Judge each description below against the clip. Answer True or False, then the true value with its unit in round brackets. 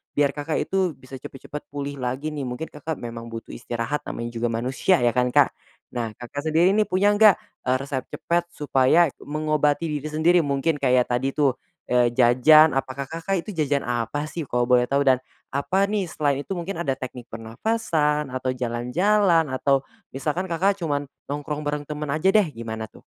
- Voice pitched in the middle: True (145 Hz)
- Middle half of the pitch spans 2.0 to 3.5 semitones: False (4.3 semitones)